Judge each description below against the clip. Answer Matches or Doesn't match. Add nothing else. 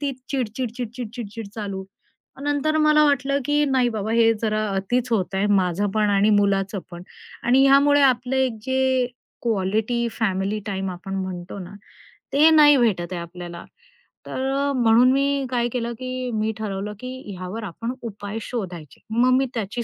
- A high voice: Matches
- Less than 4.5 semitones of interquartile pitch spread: Doesn't match